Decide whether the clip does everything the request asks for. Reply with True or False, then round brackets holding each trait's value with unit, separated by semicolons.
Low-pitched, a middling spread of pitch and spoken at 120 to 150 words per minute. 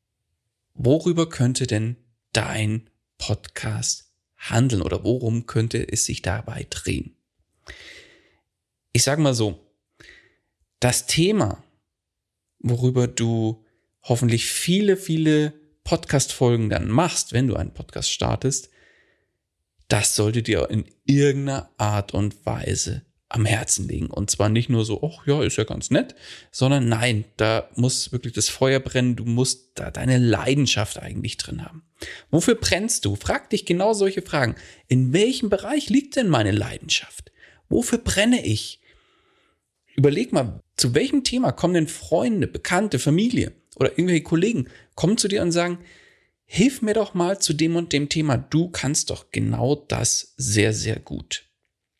False (125 Hz; 6.5 semitones; 140 wpm)